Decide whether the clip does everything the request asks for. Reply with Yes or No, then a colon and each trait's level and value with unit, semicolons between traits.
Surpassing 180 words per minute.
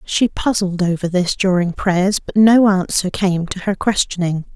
No: average, 170 wpm